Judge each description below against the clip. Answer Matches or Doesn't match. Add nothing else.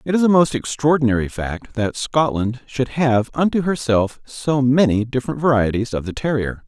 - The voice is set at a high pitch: Doesn't match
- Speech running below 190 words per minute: Matches